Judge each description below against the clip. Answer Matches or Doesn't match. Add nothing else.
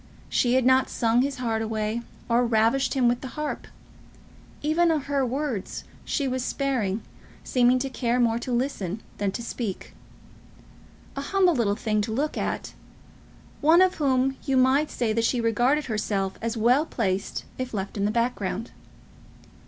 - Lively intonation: Doesn't match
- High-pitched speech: Matches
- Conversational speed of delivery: Matches